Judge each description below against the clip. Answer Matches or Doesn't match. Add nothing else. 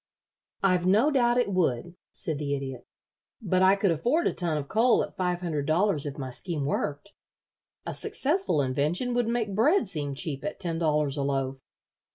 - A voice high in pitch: Doesn't match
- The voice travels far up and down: Matches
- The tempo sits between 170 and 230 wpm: Matches